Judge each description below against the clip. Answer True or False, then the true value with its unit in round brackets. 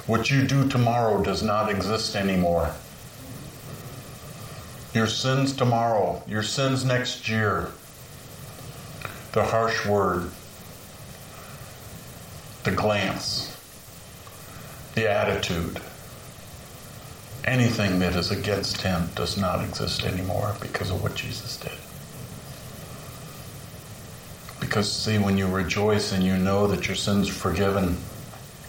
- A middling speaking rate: False (100 wpm)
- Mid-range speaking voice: False (110 Hz)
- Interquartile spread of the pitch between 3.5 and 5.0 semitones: True (4.5 semitones)